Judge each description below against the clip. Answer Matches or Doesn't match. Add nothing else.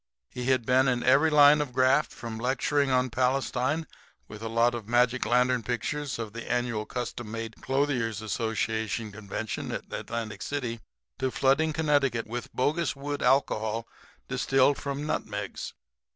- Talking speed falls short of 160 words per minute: Matches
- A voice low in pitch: Matches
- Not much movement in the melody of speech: Doesn't match